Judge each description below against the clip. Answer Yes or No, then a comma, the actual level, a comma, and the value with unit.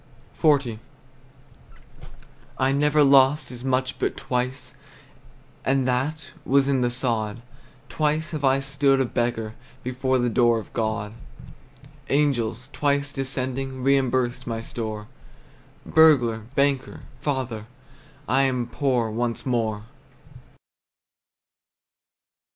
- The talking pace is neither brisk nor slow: No, slow, 105 wpm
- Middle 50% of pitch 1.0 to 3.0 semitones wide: Yes, narrow, 2.6 semitones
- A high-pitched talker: No, low, 130 Hz